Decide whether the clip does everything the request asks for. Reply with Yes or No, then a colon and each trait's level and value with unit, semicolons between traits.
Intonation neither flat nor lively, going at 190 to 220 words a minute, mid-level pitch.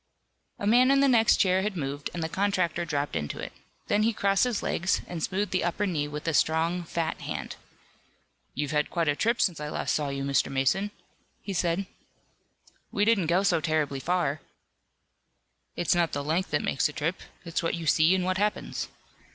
Yes: average, 4.7 semitones; average, 195 wpm; medium, 170 Hz